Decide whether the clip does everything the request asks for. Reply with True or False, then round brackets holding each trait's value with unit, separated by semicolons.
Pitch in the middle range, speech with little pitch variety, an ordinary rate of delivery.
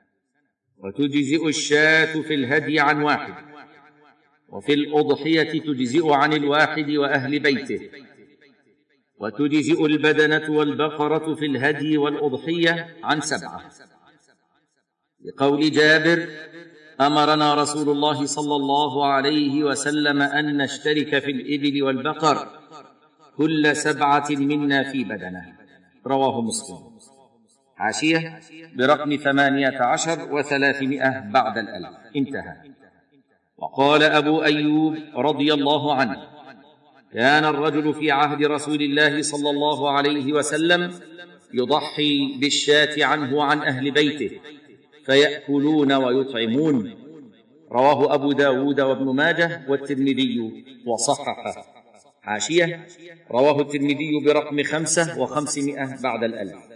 True (150 Hz; 1.3 semitones; 95 wpm)